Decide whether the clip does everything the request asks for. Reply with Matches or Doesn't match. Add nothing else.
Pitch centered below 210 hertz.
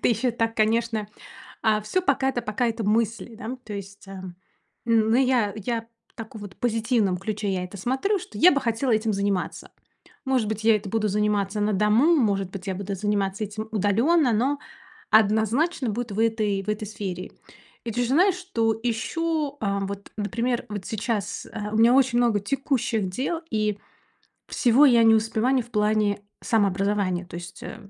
Doesn't match